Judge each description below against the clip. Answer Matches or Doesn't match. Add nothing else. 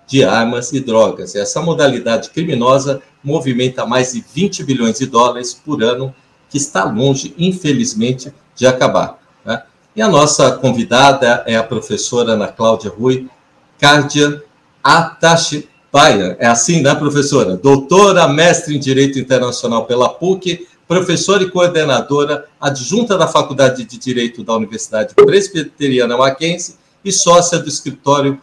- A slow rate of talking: Doesn't match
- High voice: Doesn't match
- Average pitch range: Matches